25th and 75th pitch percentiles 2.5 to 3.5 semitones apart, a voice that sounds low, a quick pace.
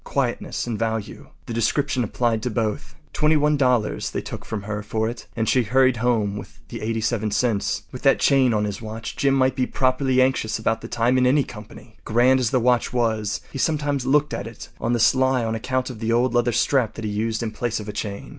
Yes: average, 2.8 semitones; low, 120 Hz; fast, 225 wpm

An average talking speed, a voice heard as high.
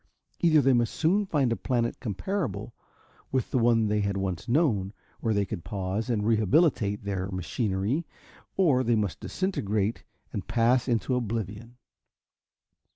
No: average, 145 wpm; low, 115 Hz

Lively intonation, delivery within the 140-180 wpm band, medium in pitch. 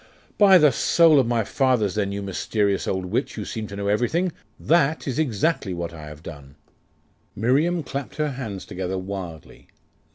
No: wide, 7.2 semitones; average, 170 wpm; low, 110 Hz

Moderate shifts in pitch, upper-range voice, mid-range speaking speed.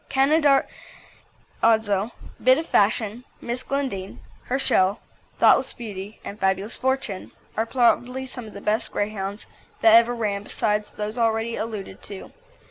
No: average, 3.5 semitones; high, 225 Hz; slow, 125 wpm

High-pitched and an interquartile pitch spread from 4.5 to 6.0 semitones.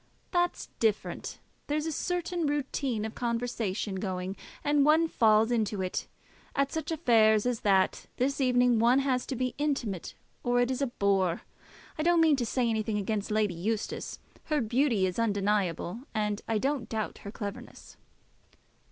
Yes: high, 230 Hz; average, 4.8 semitones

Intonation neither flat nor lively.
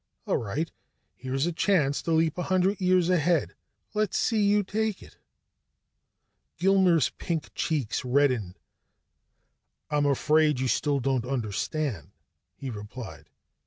No: wide, 5.7 semitones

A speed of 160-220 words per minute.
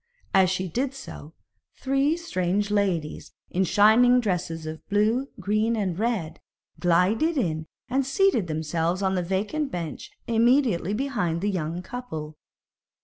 No: slow, 135 wpm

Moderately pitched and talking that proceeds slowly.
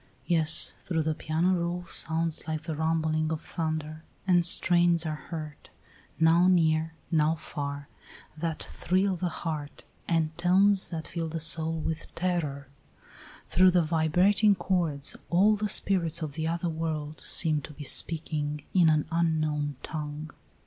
No: medium, 160 Hz; average, 145 wpm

